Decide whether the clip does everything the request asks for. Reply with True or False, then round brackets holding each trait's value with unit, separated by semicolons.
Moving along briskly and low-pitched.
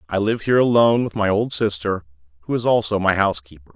True (210 wpm; 100 Hz)